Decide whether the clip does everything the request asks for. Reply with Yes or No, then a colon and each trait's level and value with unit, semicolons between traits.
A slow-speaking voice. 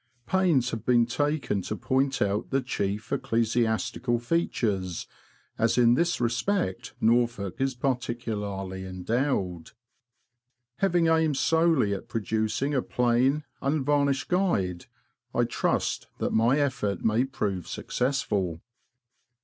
Yes: slow, 110 wpm